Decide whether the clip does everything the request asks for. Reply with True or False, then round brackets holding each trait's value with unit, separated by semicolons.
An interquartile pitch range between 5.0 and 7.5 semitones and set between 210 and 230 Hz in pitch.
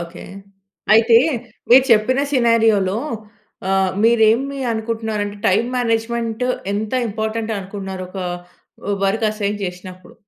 False (2.8 semitones; 220 Hz)